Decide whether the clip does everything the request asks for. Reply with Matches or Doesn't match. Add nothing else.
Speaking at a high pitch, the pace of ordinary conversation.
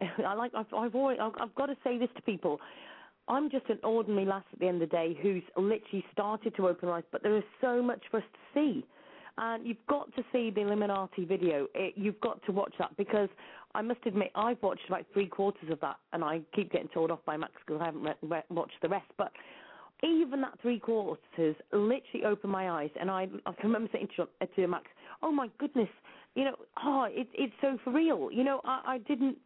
Doesn't match